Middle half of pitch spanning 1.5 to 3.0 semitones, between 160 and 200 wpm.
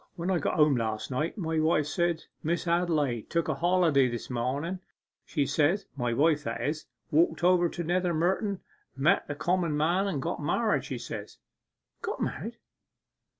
No: average, 3.7 semitones; average, 170 wpm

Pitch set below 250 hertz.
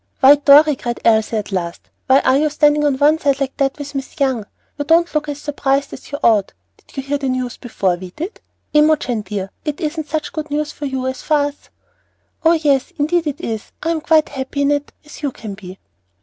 No: very high, 285 Hz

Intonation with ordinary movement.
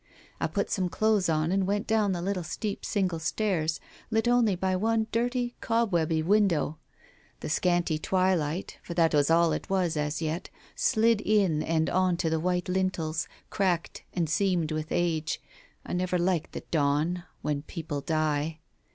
Yes: average, 3.7 semitones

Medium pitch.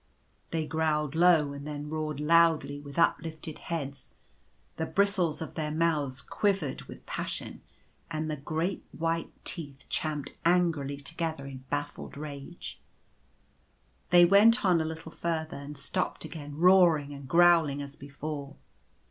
Yes: medium, 155 Hz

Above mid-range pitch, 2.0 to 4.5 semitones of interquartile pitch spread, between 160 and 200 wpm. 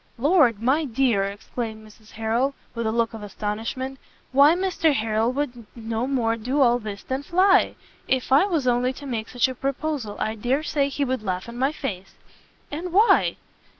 Yes: very high, 250 Hz; average, 4.1 semitones; average, 185 wpm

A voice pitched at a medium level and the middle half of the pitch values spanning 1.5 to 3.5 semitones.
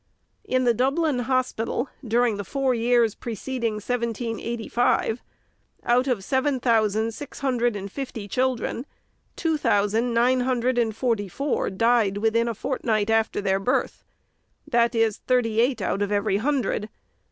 No: high, 235 Hz; average, 2.7 semitones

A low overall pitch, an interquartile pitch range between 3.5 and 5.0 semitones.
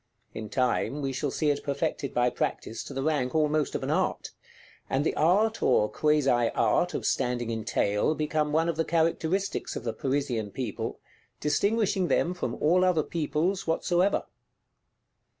No: medium, 150 Hz; average, 4.7 semitones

